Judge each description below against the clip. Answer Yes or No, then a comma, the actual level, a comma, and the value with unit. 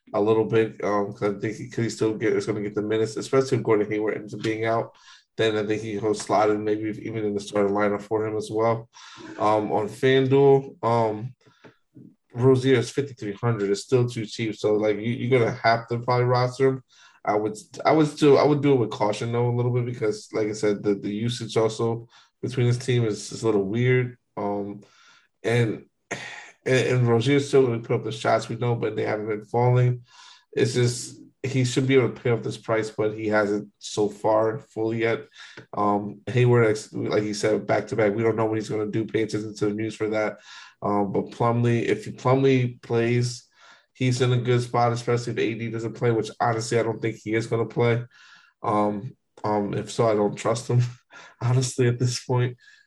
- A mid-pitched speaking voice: No, low, 115 Hz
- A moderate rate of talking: No, fast, 220 wpm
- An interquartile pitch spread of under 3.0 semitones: Yes, narrow, 2.5 semitones